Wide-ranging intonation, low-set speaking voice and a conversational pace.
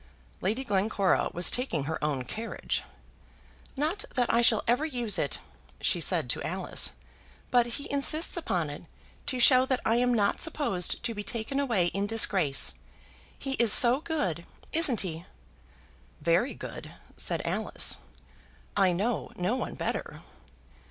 No: wide, 5.8 semitones; high, 230 Hz; average, 145 wpm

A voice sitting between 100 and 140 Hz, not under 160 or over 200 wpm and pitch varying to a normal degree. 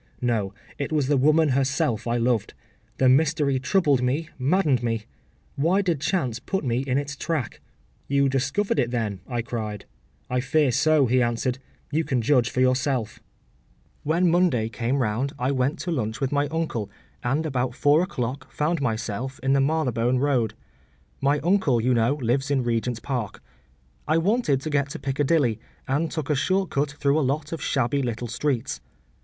Yes: low, 135 Hz; average, 175 wpm; average, 3.7 semitones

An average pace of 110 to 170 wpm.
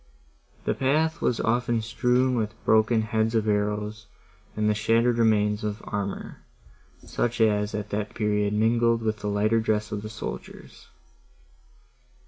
Yes: average, 145 wpm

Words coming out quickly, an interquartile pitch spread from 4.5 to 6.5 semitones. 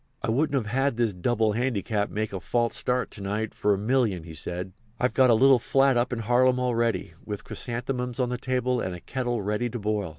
No: fast, 225 wpm; average, 3.3 semitones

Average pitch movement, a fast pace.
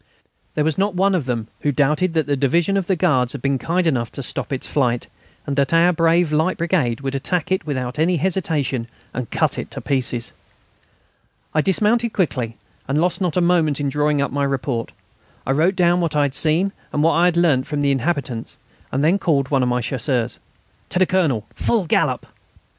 Yes: average, 4.6 semitones; fast, 210 wpm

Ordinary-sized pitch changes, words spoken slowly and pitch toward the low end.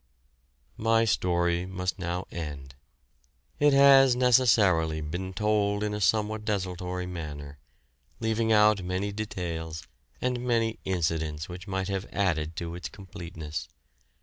Yes: average, 4.2 semitones; slow, 120 wpm; very low, 95 Hz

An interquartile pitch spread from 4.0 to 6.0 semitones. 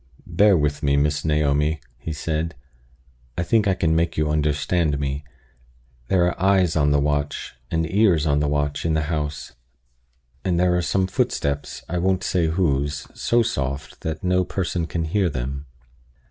No: average, 3.5 semitones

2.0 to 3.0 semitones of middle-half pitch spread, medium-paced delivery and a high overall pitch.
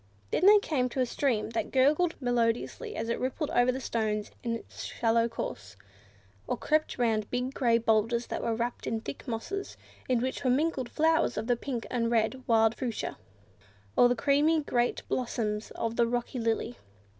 Yes: narrow, 2.6 semitones; average, 180 wpm; high, 240 Hz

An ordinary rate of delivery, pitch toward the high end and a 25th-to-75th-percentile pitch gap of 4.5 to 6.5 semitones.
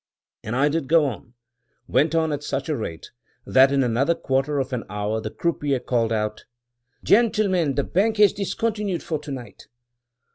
No: average, 180 wpm; medium, 140 Hz; wide, 5.5 semitones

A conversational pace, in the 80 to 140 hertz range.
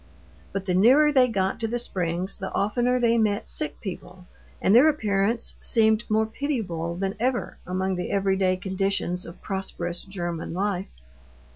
No: average, 155 wpm; high, 195 Hz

